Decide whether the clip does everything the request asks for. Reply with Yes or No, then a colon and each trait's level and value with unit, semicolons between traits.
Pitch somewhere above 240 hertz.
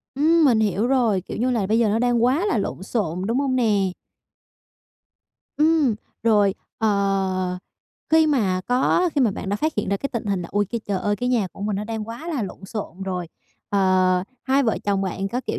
No: high, 215 Hz